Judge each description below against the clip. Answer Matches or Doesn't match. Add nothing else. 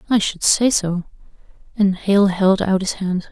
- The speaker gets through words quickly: Doesn't match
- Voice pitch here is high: Matches